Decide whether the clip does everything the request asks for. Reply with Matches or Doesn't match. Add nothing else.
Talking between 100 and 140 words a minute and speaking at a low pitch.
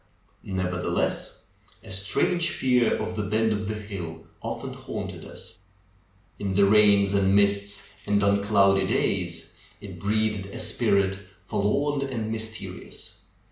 Matches